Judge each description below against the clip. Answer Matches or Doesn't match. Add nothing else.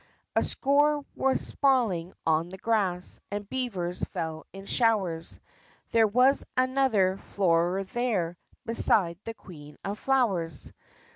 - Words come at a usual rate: Doesn't match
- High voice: Matches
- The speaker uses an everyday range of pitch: Doesn't match